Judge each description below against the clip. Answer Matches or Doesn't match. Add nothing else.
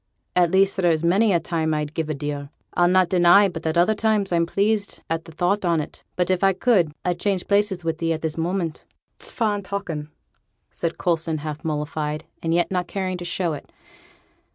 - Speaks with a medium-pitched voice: Matches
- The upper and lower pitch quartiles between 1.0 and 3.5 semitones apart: Matches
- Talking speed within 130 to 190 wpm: Doesn't match